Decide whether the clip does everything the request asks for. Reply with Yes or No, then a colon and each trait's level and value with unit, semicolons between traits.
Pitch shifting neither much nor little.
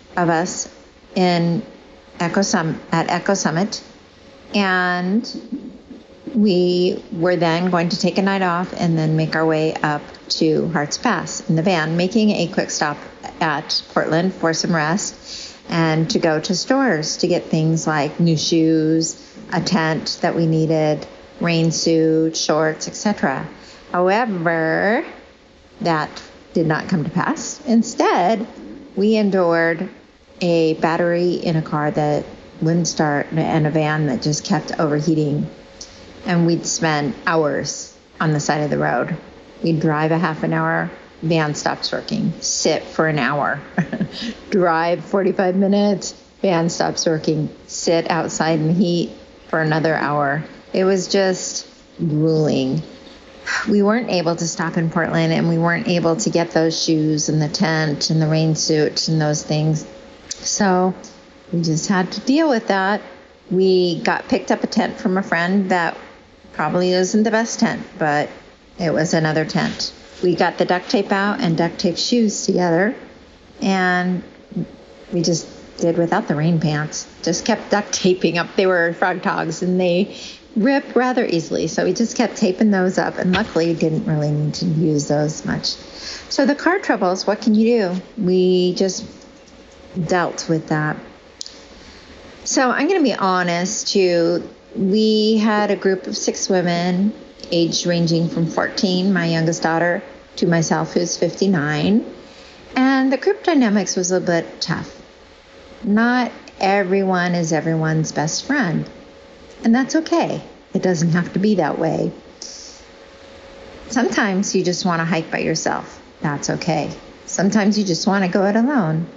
Yes: average, 3.7 semitones